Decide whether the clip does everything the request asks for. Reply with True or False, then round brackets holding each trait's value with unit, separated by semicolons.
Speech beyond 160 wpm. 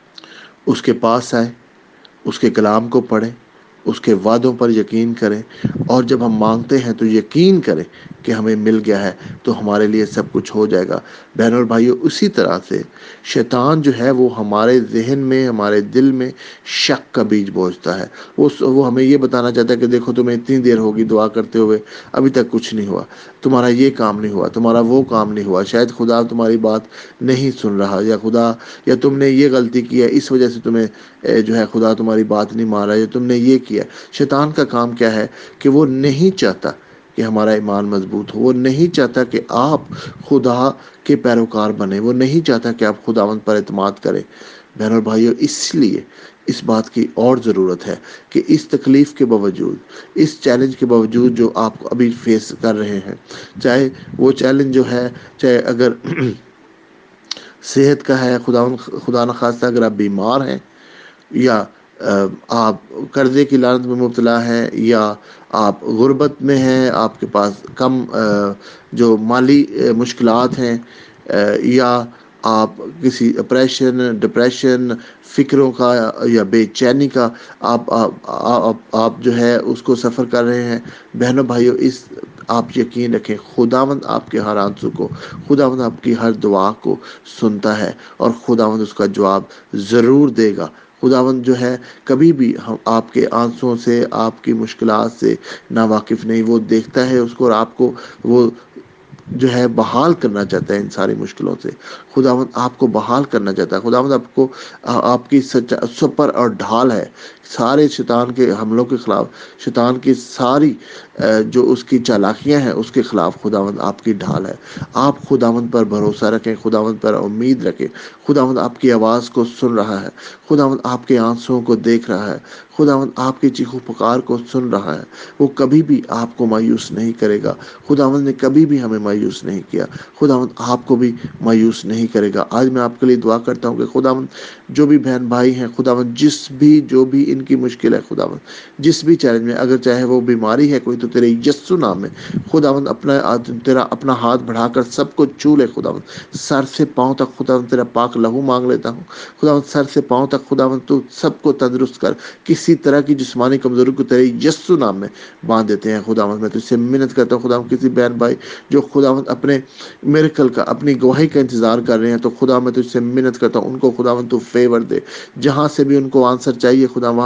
True (190 wpm)